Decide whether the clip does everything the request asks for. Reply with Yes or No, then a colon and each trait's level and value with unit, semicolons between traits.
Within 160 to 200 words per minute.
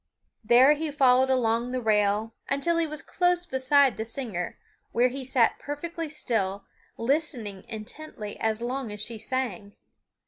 No: average, 145 wpm